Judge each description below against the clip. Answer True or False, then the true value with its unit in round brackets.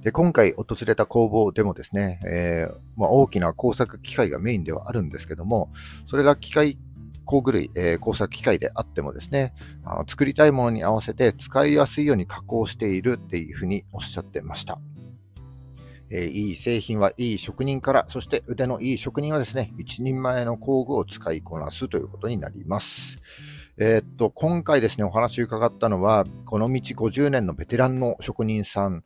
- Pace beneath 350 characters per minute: False (375 characters per minute)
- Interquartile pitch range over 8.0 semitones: False (5.6 semitones)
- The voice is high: False (110 Hz)